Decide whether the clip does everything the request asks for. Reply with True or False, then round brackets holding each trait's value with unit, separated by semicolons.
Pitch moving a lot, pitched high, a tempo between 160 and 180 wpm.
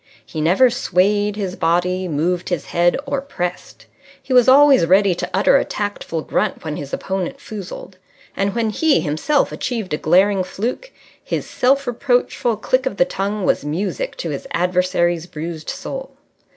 True (6.2 semitones; 195 Hz; 165 wpm)